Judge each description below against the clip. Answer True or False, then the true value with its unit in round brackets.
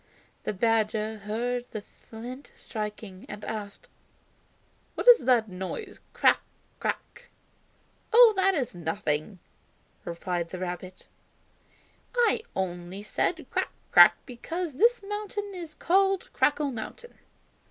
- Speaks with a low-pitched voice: False (225 Hz)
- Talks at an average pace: False (110 wpm)